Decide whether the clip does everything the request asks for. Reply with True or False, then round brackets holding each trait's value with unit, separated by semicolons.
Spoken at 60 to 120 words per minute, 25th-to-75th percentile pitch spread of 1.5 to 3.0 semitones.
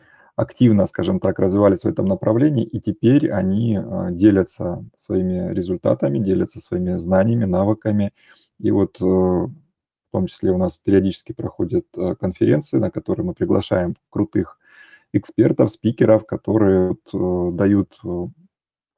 True (115 wpm; 2.7 semitones)